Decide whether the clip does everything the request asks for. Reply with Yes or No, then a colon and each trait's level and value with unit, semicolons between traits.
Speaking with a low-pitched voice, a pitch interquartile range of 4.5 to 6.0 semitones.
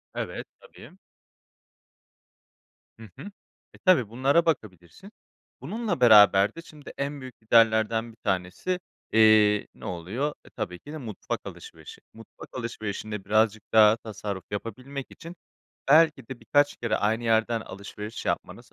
Yes: low, 115 Hz; average, 4.8 semitones